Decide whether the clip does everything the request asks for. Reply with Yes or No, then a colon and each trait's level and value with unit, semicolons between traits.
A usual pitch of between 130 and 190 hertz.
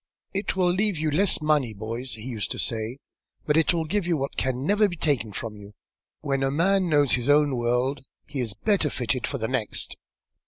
Yes: medium, 140 Hz